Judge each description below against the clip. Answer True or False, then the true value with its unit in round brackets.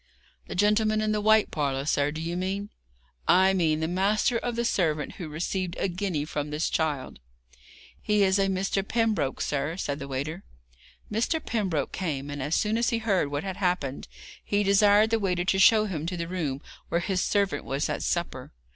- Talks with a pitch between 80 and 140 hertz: False (185 Hz)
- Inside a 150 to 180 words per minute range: False (195 wpm)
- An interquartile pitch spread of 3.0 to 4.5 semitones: False (5.2 semitones)